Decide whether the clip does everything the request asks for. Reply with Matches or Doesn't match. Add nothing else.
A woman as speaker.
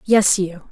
Matches